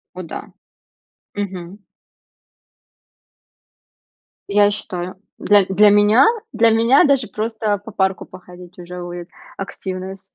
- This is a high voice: Yes, high, 195 Hz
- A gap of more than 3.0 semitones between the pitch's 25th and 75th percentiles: No, average, 2.7 semitones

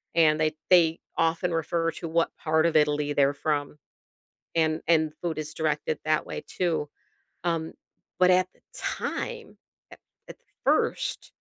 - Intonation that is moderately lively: No, narrow, 1.6 semitones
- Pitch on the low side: No, medium, 160 Hz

